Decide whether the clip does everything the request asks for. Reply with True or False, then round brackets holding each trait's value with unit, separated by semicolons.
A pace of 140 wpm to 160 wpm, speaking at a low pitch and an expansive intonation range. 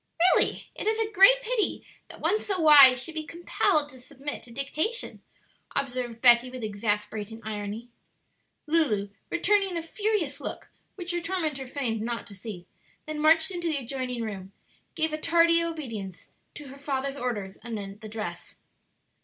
False (155 wpm; 275 Hz; 6.7 semitones)